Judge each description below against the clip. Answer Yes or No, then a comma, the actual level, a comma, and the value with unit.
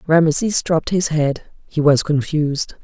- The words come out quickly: No, average, 150 wpm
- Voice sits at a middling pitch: Yes, medium, 155 Hz